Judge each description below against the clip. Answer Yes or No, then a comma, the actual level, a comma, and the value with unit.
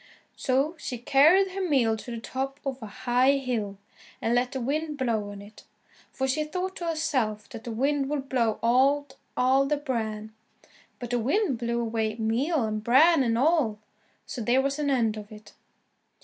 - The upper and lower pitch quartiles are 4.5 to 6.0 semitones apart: No, average, 4.1 semitones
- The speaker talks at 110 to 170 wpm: No, average, 185 wpm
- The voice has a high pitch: Yes, very high, 255 Hz